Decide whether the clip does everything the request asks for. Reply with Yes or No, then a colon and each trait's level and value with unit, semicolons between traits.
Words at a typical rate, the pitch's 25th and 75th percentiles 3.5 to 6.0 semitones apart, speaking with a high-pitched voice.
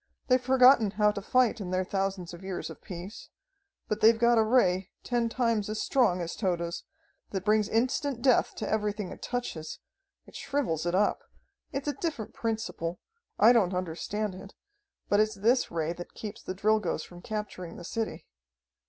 Yes: average, 175 wpm; average, 4.1 semitones; high, 210 Hz